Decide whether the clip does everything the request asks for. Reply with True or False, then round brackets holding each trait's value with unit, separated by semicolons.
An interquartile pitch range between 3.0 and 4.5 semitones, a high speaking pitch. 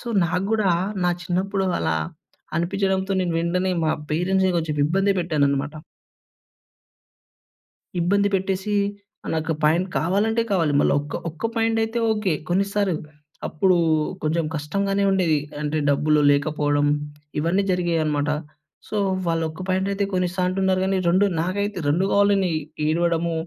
False (3.7 semitones; 180 Hz)